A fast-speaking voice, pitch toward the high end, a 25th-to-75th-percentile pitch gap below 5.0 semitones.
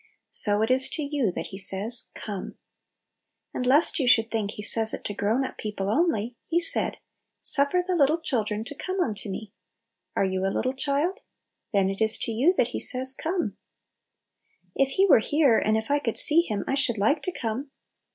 No: fast, 225 wpm; high, 245 Hz; wide, 5.4 semitones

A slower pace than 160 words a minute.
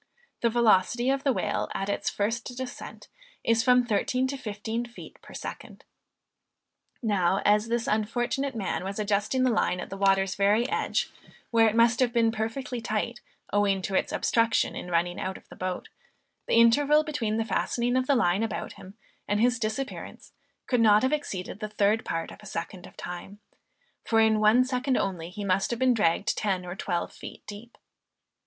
No: average, 185 wpm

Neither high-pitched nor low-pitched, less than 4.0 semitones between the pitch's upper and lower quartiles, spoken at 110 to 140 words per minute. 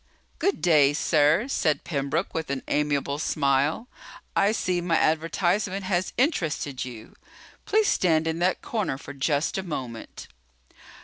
No: medium, 160 Hz; average, 4.6 semitones; slow, 135 wpm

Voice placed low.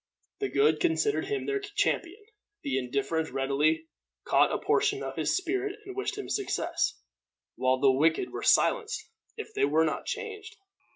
No: very high, 385 Hz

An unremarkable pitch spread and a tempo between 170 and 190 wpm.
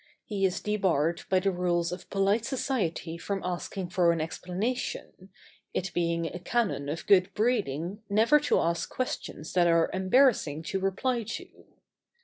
No: average, 3.7 semitones; average, 150 wpm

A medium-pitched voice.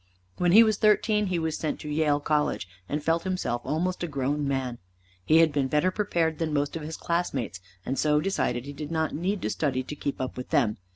Yes: medium, 155 Hz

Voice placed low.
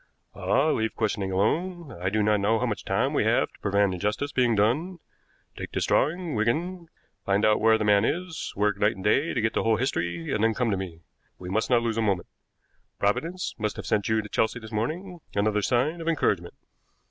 Yes: low, 110 Hz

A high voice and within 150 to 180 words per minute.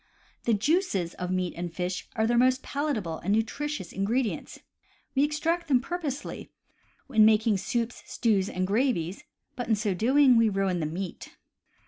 Yes: high, 220 Hz; average, 155 wpm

